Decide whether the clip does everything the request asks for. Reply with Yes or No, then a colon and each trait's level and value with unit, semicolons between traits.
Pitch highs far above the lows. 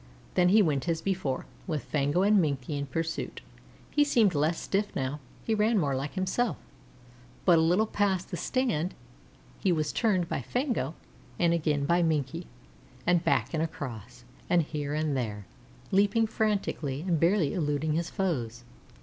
No: average, 5.0 semitones